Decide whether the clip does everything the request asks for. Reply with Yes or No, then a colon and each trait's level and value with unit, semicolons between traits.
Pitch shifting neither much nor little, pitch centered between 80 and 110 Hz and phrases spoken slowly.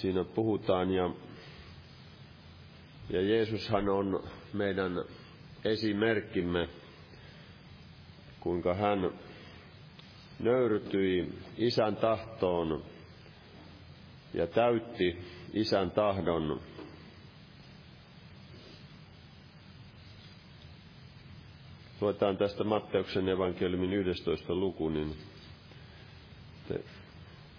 Yes: average, 3.2 semitones; very low, 95 Hz; slow, 50 wpm